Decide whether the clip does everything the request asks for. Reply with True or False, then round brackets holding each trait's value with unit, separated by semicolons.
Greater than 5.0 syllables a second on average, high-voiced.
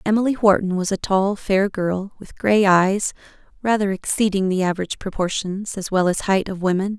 True (5.2 syllables/s; 195 Hz)